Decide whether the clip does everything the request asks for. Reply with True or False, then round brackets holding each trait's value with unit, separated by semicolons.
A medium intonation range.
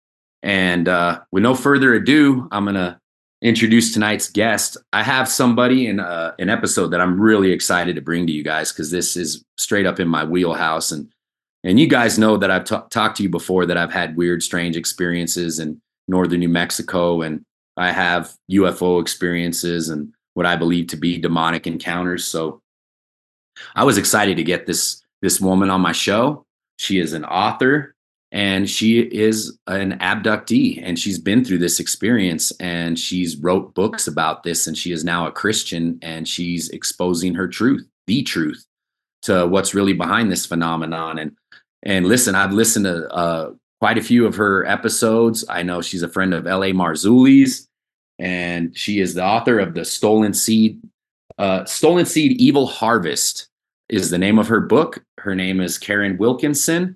True (3.8 semitones)